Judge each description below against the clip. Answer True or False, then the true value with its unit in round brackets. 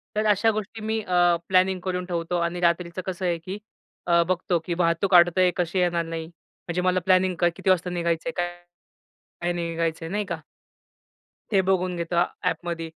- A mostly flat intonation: True (1.5 semitones)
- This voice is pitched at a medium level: True (175 Hz)